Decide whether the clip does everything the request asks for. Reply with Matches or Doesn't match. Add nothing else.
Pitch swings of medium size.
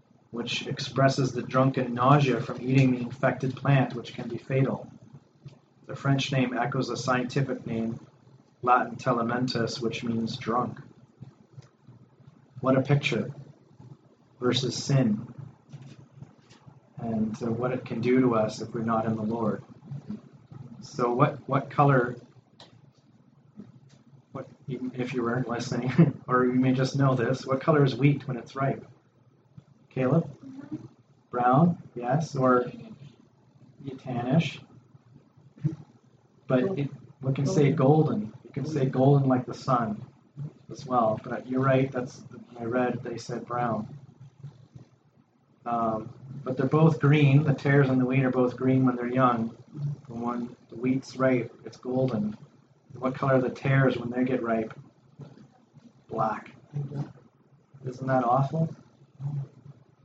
Doesn't match